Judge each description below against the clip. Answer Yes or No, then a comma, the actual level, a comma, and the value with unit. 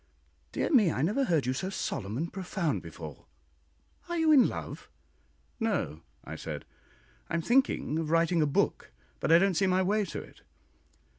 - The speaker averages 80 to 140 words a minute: No, average, 175 wpm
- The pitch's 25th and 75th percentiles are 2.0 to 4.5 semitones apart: No, wide, 5.5 semitones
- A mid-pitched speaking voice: Yes, medium, 170 Hz